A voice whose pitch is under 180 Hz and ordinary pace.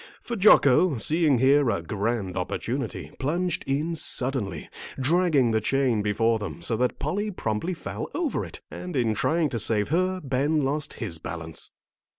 Yes: low, 135 Hz; average, 160 wpm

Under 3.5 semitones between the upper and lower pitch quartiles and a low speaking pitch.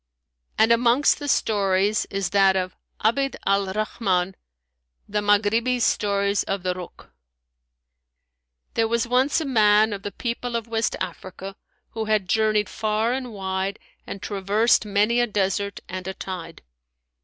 No: average, 2.8 semitones; high, 210 Hz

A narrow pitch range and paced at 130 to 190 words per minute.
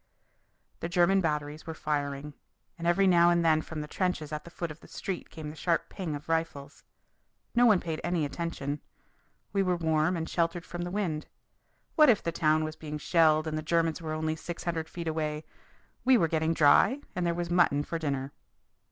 No: narrow, 2.2 semitones; fast, 205 wpm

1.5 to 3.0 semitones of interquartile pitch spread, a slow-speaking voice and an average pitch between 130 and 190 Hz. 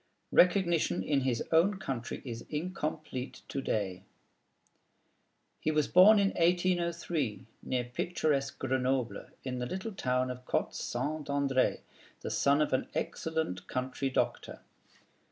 No: average, 5.1 semitones; slow, 125 wpm; medium, 140 Hz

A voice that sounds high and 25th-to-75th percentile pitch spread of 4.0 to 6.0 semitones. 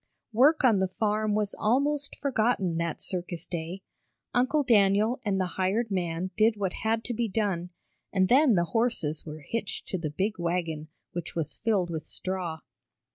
Yes: high, 195 Hz; average, 4.6 semitones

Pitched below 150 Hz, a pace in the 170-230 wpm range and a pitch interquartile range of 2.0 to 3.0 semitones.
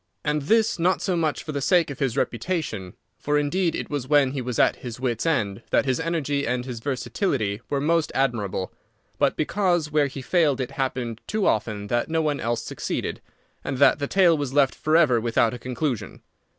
No: medium, 140 Hz; average, 190 wpm; average, 4.6 semitones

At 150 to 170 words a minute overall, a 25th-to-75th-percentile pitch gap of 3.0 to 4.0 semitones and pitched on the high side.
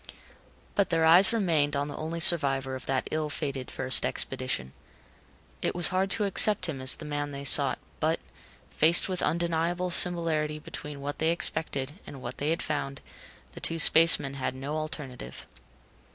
No: average, 165 wpm; average, 3.4 semitones; medium, 150 Hz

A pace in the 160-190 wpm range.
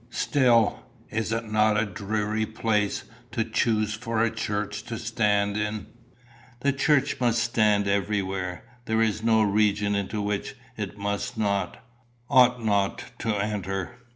No: average, 145 wpm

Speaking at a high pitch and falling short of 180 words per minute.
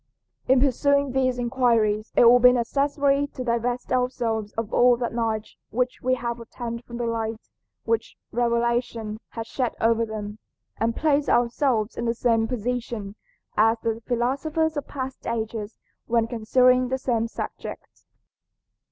Yes: high, 235 Hz; average, 145 wpm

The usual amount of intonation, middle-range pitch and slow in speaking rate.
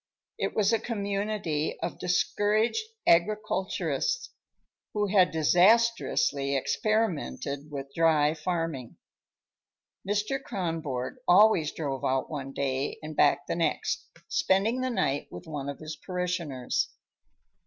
No: wide, 6.5 semitones; medium, 170 Hz; slow, 110 wpm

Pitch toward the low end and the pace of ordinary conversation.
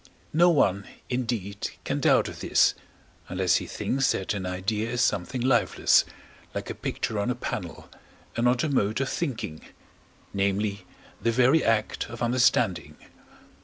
Yes: low, 115 Hz; average, 150 wpm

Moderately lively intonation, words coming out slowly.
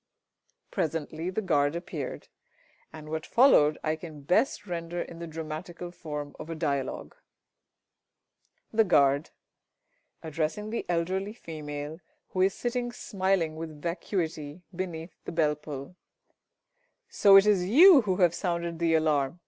Yes: average, 3.3 semitones; slow, 130 wpm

